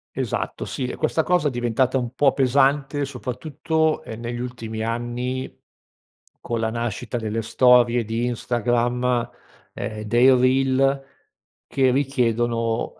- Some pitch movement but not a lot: No, narrow, 2.3 semitones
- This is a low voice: Yes, low, 125 Hz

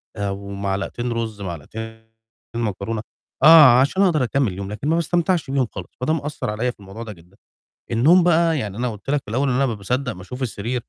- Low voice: Yes, low, 115 Hz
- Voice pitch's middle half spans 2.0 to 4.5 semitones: No, wide, 5.4 semitones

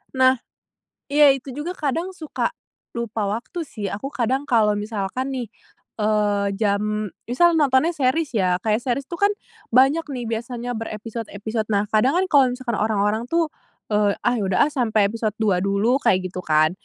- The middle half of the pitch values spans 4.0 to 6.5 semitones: Yes, average, 4.3 semitones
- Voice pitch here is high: Yes, high, 230 Hz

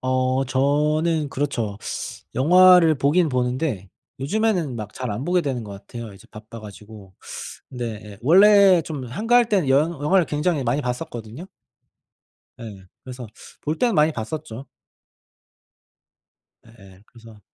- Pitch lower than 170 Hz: Yes, low, 135 Hz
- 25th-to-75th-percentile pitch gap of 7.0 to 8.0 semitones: No, wide, 5.9 semitones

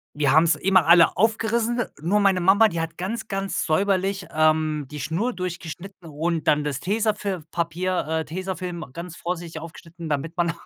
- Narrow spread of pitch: No, average, 3.4 semitones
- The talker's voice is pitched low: No, medium, 175 Hz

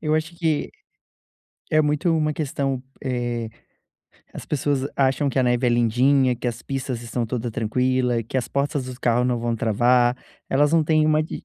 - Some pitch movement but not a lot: Yes, average, 3.4 semitones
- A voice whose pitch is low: Yes, low, 130 Hz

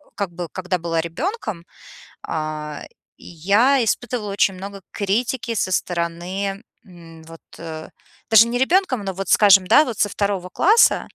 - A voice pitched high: Yes, high, 195 Hz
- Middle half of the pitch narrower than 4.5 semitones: No, average, 4.9 semitones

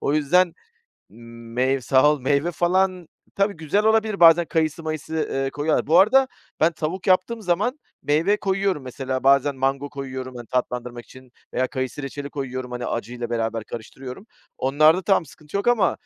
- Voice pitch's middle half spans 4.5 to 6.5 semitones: Yes, wide, 5.6 semitones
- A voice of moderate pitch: Yes, medium, 145 Hz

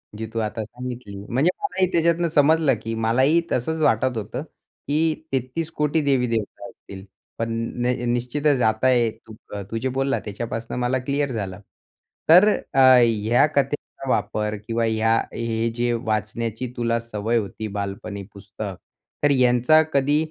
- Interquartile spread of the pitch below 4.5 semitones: Yes, average, 3.8 semitones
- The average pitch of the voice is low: Yes, low, 120 Hz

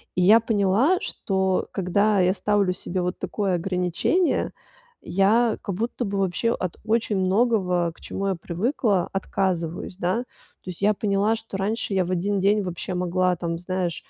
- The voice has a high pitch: Yes, high, 195 Hz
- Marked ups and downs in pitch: No, average, 2.7 semitones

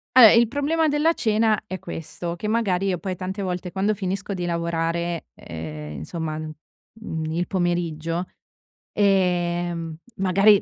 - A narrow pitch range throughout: No, average, 3.5 semitones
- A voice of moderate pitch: Yes, medium, 180 Hz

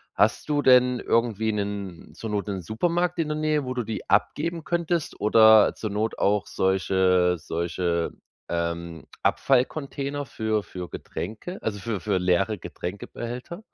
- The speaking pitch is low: Yes, low, 110 Hz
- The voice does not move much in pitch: No, wide, 6.3 semitones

